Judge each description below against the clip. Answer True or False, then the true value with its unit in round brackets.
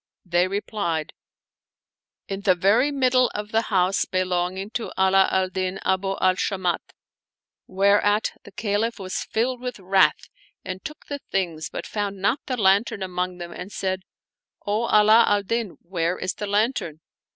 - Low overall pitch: False (195 Hz)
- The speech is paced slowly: False (165 wpm)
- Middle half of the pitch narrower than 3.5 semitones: True (2.7 semitones)